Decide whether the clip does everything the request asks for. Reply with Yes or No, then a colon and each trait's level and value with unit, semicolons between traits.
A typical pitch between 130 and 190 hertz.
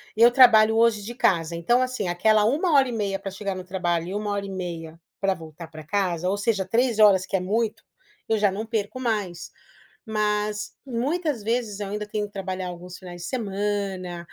No: high, 205 Hz